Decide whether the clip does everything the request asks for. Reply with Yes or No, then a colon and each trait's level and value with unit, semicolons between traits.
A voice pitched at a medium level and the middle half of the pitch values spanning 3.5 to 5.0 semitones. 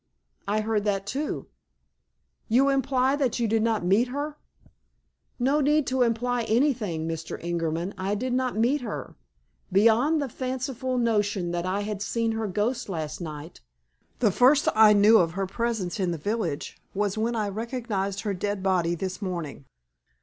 No: high, 215 Hz; average, 4.6 semitones